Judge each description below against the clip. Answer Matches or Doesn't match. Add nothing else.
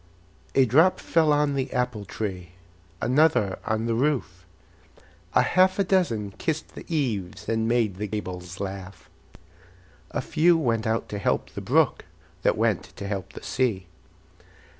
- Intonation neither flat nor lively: Doesn't match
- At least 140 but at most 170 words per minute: Matches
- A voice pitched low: Matches